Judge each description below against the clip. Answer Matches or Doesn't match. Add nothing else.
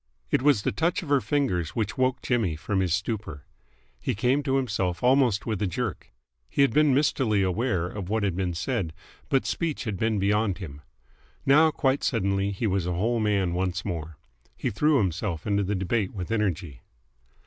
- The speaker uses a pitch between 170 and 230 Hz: Doesn't match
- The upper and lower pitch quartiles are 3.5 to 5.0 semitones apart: Doesn't match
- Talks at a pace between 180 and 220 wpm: Matches